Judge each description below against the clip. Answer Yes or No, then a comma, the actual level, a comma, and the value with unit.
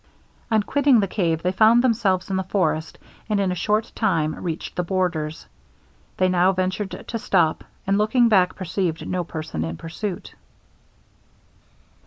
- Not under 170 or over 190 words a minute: No, average, 155 wpm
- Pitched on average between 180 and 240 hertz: Yes, medium, 185 Hz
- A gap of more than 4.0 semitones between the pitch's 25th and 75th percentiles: No, average, 3.7 semitones